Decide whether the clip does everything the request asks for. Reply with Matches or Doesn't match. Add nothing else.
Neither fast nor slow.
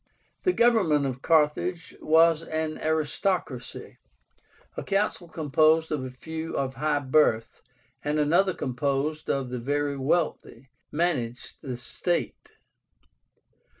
Doesn't match